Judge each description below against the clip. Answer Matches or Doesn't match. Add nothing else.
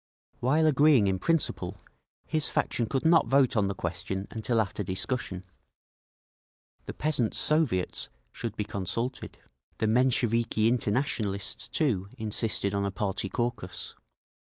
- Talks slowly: Matches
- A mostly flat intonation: Doesn't match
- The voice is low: Matches